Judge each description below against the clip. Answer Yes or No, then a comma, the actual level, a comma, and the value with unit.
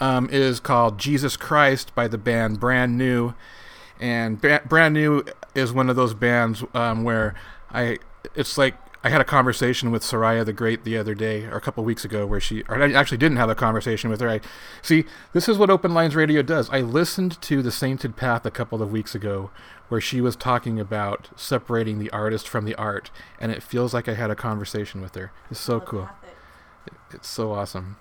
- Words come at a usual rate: No, fast, 215 wpm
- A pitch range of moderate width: Yes, average, 3.4 semitones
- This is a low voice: Yes, low, 120 Hz